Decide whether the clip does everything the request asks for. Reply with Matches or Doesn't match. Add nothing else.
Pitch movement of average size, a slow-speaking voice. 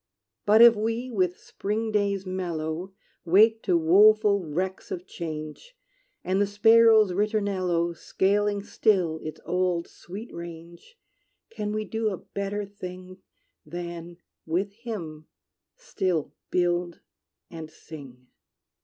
Matches